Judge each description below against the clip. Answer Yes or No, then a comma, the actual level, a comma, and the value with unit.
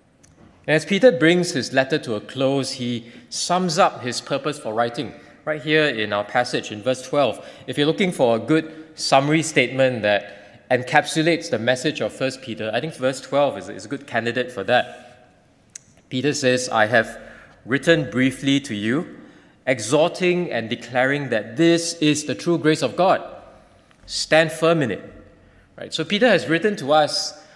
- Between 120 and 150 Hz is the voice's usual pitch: Yes, medium, 140 Hz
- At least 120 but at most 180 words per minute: Yes, average, 170 wpm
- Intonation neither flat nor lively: Yes, average, 4.3 semitones